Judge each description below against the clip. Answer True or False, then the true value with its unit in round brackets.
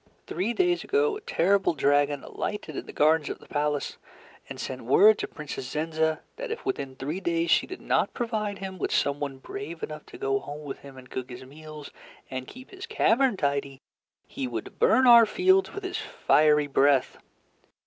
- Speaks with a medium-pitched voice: True (160 Hz)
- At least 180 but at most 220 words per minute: True (190 wpm)